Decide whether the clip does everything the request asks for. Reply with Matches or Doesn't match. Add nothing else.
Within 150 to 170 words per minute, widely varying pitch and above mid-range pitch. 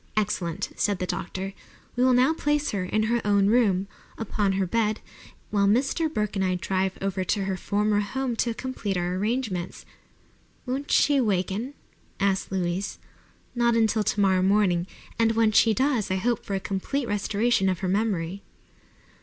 Doesn't match